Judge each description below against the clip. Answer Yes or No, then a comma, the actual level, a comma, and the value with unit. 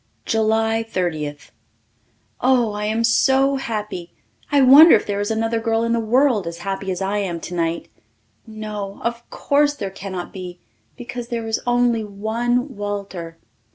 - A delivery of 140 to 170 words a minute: Yes, average, 155 wpm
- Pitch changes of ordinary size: Yes, average, 3.5 semitones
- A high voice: Yes, high, 220 Hz